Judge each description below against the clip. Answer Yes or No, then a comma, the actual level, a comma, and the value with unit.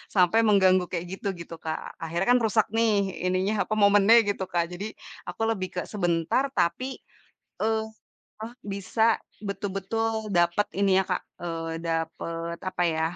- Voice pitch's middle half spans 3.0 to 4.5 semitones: Yes, average, 4.0 semitones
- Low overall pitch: No, high, 195 Hz